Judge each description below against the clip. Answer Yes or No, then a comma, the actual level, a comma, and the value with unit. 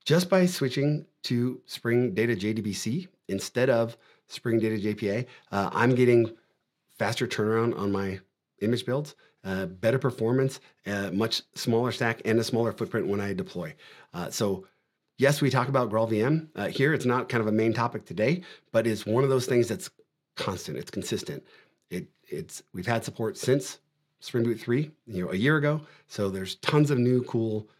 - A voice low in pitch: Yes, low, 120 Hz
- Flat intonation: No, average, 3.8 semitones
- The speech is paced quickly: No, average, 175 wpm